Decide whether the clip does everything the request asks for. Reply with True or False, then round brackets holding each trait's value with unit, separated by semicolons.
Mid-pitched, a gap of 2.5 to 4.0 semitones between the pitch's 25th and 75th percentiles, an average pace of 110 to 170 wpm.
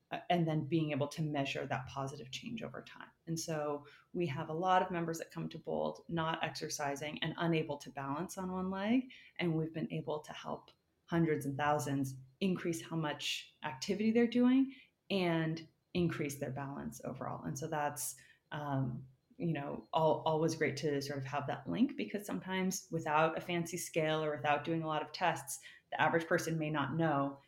False (155 Hz; 2.8 semitones; 190 wpm)